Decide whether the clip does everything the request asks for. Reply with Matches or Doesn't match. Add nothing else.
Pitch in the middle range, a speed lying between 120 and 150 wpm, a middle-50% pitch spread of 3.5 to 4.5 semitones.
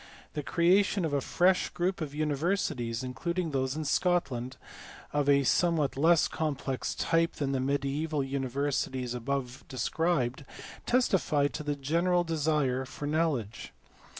Matches